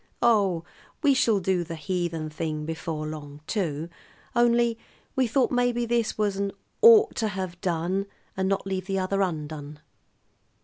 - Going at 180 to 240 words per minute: No, average, 145 wpm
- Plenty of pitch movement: Yes, wide, 5.8 semitones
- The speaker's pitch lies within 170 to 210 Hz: Yes, high, 190 Hz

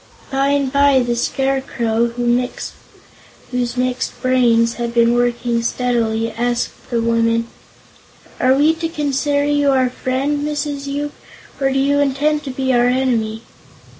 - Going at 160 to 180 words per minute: No, slow, 135 wpm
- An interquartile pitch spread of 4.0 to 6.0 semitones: No, average, 2.9 semitones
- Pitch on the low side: No, very high, 255 Hz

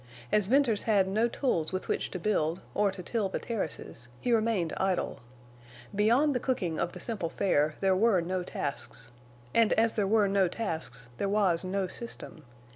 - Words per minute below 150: No, average, 180 wpm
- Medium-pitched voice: No, high, 195 Hz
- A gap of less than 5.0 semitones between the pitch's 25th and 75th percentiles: Yes, average, 4.2 semitones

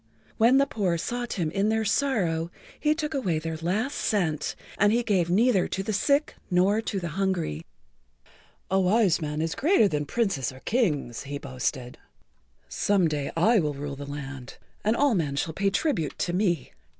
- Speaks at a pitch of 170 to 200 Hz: Yes, medium, 185 Hz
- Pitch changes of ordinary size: No, wide, 6.5 semitones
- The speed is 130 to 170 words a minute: No, average, 185 wpm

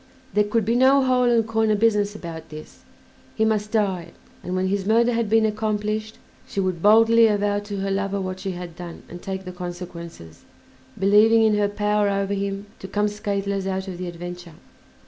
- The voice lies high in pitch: Yes, high, 200 Hz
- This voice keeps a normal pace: Yes, average, 190 wpm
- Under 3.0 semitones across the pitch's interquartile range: Yes, narrow, 2.6 semitones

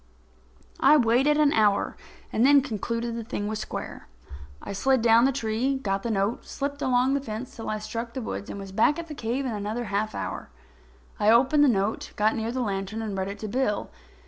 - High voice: Yes, high, 230 Hz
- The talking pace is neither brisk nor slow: No, fast, 220 wpm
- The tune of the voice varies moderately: Yes, average, 3.8 semitones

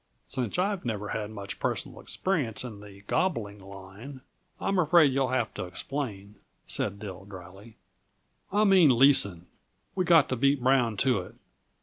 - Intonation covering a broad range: Yes, wide, 5.9 semitones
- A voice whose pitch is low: Yes, low, 115 Hz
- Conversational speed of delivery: Yes, average, 155 wpm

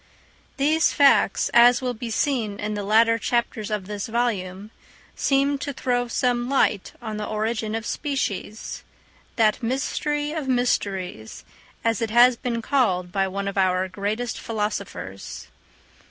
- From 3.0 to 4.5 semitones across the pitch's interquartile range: Yes, average, 3.6 semitones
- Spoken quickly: No, average, 140 wpm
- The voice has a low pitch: No, high, 225 Hz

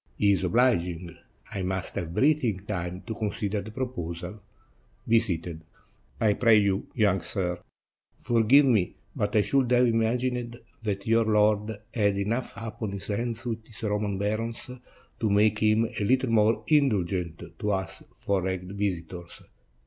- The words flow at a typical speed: Yes, average, 150 wpm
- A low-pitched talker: Yes, low, 105 Hz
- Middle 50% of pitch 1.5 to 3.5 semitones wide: Yes, average, 3.2 semitones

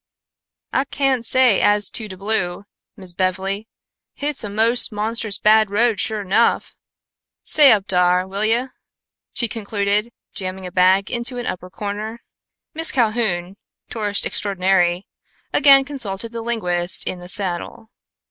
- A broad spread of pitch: No, average, 3.6 semitones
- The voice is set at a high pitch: Yes, high, 210 Hz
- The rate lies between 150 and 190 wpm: No, average, 140 wpm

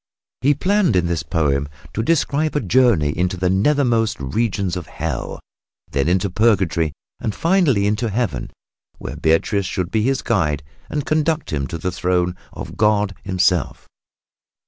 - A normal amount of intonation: No, wide, 6.2 semitones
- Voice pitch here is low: Yes, very low, 95 Hz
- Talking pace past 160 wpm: No, average, 150 wpm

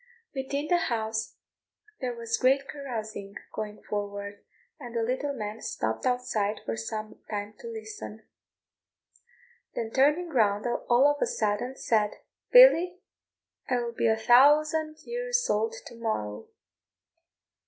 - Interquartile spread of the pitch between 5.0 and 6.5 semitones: Yes, wide, 5.4 semitones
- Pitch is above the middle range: Yes, high, 240 Hz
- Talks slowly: Yes, slow, 130 wpm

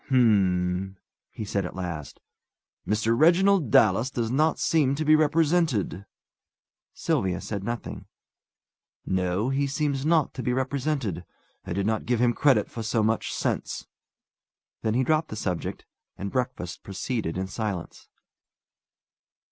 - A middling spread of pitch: No, wide, 6.5 semitones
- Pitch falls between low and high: No, low, 115 Hz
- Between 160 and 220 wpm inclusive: No, slow, 135 wpm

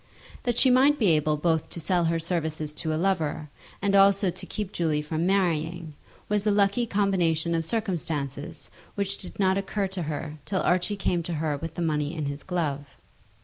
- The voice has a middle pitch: Yes, medium, 170 Hz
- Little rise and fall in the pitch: No, average, 4.0 semitones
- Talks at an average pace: Yes, average, 190 wpm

